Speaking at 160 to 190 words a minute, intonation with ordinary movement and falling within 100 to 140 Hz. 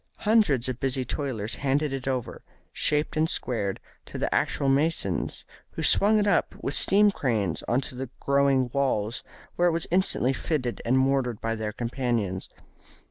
Yes: average, 165 wpm; average, 3.8 semitones; low, 135 Hz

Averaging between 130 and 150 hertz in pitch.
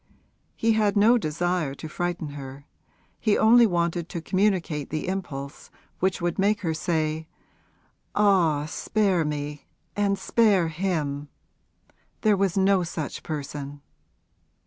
No: medium, 175 Hz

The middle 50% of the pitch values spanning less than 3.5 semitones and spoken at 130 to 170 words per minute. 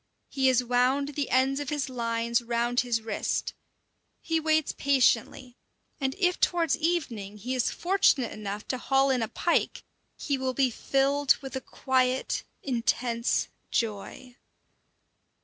Yes: average, 3.0 semitones; average, 140 wpm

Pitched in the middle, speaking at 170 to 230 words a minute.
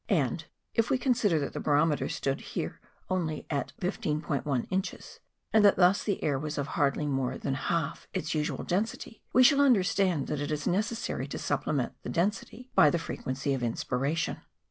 Yes: medium, 160 Hz; average, 175 wpm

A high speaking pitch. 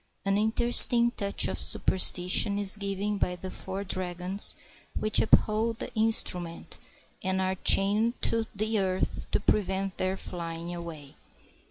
Yes: high, 195 Hz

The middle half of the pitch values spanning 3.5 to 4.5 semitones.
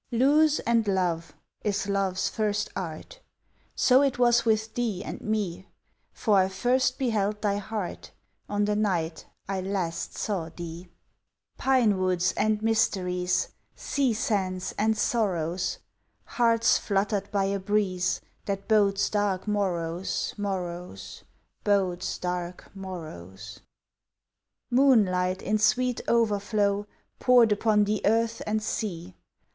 No: average, 3.1 semitones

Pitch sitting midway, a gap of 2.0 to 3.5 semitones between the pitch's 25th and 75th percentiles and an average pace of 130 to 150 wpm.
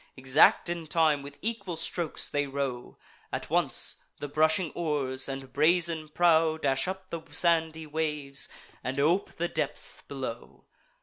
Yes: medium, 155 Hz; average, 3.1 semitones; average, 140 wpm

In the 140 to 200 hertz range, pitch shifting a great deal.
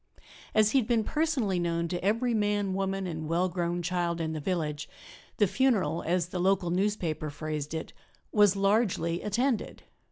No: medium, 185 Hz; average, 3.7 semitones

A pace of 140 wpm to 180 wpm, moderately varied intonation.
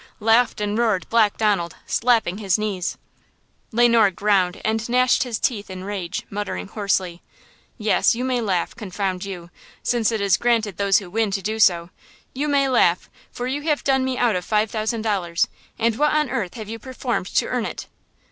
No: average, 190 wpm; average, 3.8 semitones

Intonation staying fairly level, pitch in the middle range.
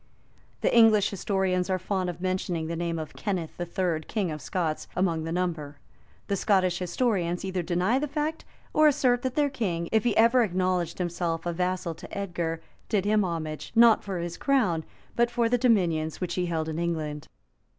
No: average, 4.1 semitones; medium, 180 Hz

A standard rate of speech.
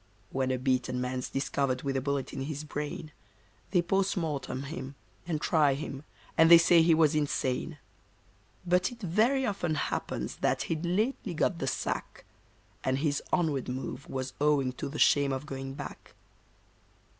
Yes: average, 165 wpm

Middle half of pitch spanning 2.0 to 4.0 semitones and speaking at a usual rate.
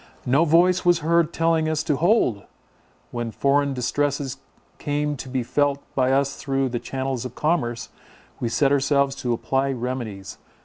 Yes: average, 2.9 semitones; average, 160 wpm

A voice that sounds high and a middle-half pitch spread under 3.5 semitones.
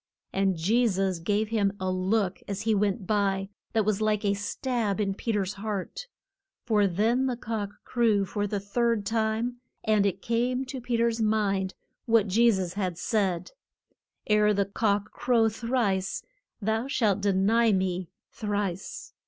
Yes: high, 210 Hz; narrow, 2.6 semitones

